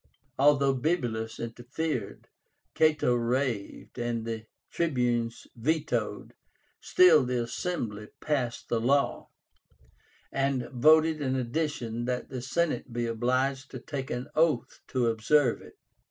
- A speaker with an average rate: No, slow, 115 wpm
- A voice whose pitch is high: No, low, 130 Hz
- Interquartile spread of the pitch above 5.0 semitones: No, average, 3.9 semitones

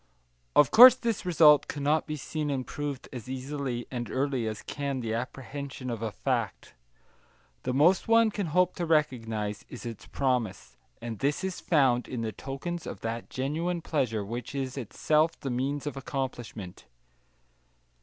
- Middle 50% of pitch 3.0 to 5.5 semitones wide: Yes, average, 4.0 semitones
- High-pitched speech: No, low, 135 Hz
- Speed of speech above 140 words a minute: Yes, average, 160 wpm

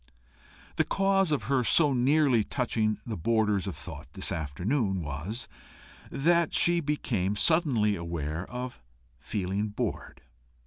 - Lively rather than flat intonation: Yes, wide, 6.7 semitones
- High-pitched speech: No, low, 110 Hz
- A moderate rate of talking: No, slow, 125 wpm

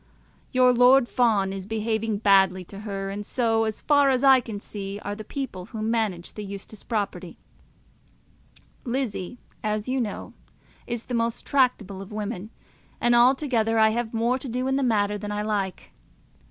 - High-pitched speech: Yes, high, 220 Hz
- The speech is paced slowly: No, average, 175 wpm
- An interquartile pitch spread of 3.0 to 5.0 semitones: Yes, average, 3.4 semitones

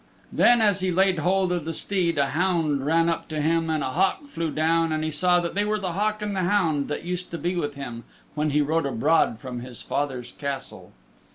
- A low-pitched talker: No, medium, 165 Hz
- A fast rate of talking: Yes, fast, 235 wpm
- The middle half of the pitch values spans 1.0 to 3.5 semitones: No, average, 4.0 semitones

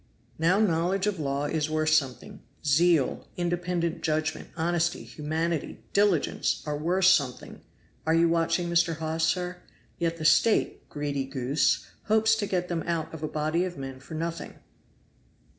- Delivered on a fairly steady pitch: Yes, narrow, 2.3 semitones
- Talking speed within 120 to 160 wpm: Yes, average, 150 wpm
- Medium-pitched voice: Yes, medium, 165 Hz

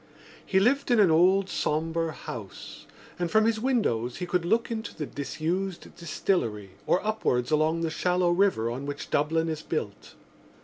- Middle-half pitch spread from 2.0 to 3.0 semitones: No, average, 4.8 semitones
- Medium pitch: Yes, medium, 165 Hz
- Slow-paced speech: No, average, 165 wpm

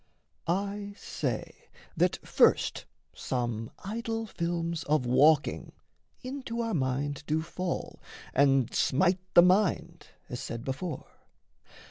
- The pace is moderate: No, slow, 105 wpm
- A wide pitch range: Yes, wide, 6.4 semitones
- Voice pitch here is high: No, medium, 170 Hz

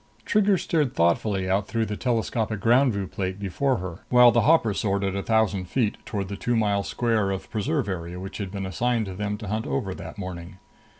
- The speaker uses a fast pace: Yes, fast, 215 wpm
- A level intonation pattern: No, average, 3.4 semitones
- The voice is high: No, low, 100 Hz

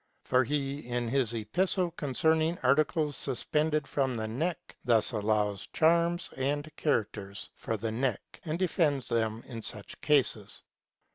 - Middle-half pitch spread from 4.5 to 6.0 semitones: Yes, wide, 5.5 semitones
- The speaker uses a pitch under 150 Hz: Yes, low, 135 Hz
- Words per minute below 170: Yes, slow, 135 wpm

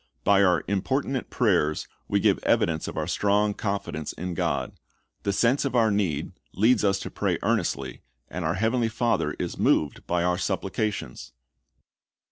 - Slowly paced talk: No, average, 155 wpm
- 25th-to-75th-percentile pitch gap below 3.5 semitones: No, average, 4.2 semitones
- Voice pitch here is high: No, low, 100 Hz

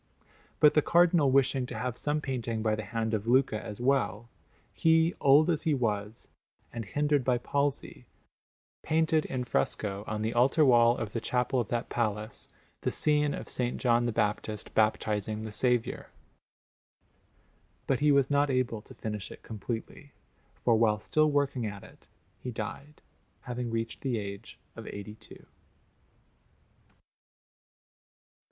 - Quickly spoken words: No, average, 150 wpm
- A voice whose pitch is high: No, low, 120 Hz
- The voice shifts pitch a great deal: No, average, 4.4 semitones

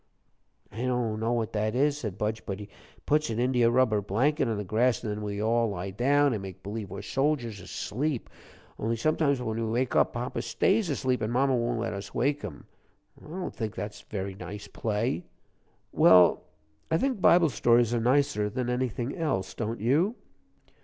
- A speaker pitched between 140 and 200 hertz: No, low, 115 Hz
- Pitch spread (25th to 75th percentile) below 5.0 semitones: Yes, average, 3.9 semitones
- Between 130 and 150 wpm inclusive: No, average, 190 wpm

